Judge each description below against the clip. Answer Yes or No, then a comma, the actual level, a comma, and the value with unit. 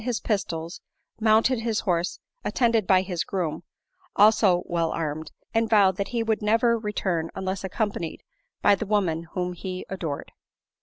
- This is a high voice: Yes, high, 195 Hz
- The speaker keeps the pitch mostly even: No, average, 4.0 semitones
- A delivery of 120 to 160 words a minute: Yes, average, 155 wpm